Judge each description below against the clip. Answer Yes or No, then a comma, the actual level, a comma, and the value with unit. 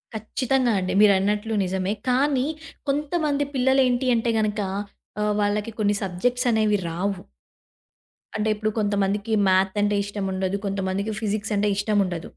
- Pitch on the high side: Yes, high, 210 Hz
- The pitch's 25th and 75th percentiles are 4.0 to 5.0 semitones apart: No, average, 3.3 semitones